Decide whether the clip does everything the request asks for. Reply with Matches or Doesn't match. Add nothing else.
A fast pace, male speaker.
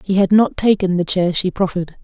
Doesn't match